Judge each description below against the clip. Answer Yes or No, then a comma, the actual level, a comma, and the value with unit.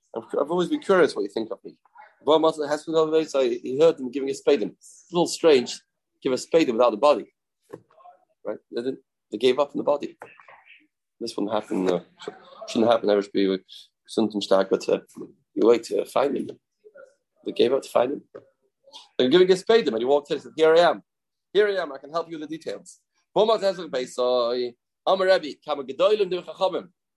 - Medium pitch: Yes, medium, 175 Hz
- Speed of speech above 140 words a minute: Yes, fast, 205 wpm